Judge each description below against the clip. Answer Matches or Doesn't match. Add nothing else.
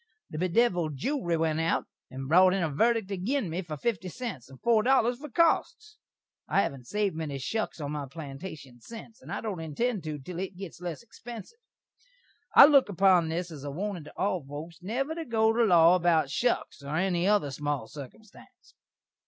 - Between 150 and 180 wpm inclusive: Doesn't match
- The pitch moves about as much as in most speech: Doesn't match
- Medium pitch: Matches